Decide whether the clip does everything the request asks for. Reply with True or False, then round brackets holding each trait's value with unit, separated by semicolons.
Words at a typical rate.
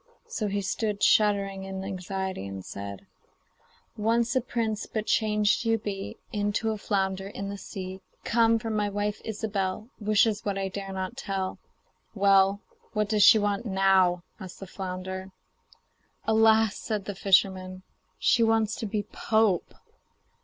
True (145 wpm)